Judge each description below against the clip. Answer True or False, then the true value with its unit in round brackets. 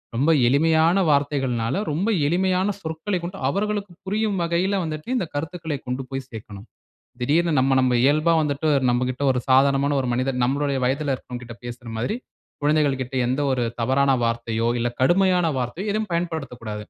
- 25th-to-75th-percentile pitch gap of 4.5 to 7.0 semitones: True (5.1 semitones)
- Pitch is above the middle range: False (140 Hz)